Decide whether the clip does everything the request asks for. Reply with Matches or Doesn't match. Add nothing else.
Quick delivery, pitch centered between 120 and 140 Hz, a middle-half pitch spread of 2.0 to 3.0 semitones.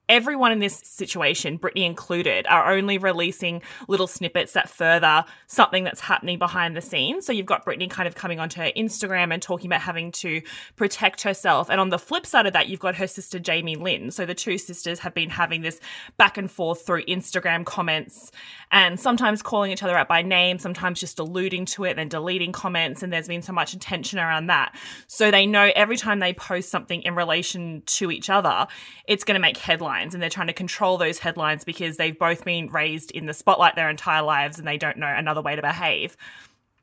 Doesn't match